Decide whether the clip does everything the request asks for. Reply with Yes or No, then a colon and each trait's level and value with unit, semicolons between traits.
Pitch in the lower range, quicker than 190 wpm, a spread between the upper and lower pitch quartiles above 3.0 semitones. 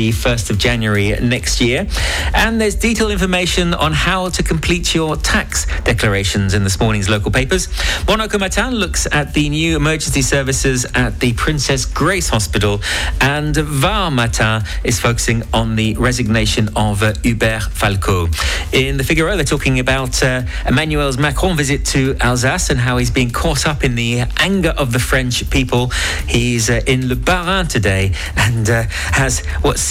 No: low, 125 Hz; average, 165 wpm; wide, 5.6 semitones